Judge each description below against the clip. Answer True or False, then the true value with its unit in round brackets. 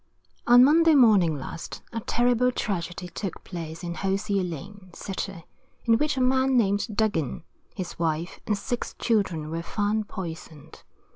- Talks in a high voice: True (200 Hz)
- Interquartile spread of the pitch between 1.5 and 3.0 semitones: False (5.5 semitones)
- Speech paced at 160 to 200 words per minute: False (145 wpm)